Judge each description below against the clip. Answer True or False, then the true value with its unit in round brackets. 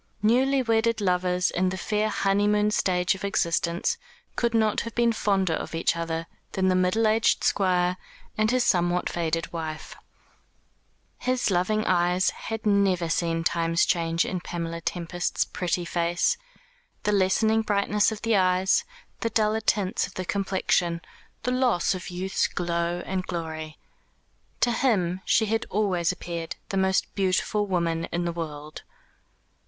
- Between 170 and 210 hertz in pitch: True (185 Hz)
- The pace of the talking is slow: False (150 wpm)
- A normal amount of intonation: True (3.6 semitones)